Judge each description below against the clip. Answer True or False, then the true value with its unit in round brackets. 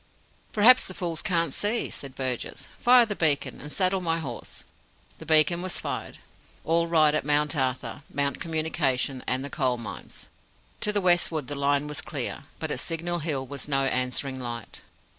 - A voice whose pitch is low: False (150 Hz)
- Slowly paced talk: False (175 wpm)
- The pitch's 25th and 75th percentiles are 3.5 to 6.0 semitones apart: True (3.9 semitones)